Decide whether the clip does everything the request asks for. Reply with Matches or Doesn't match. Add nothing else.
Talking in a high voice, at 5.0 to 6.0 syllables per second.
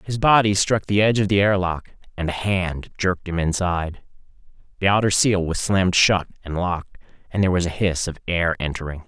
Doesn't match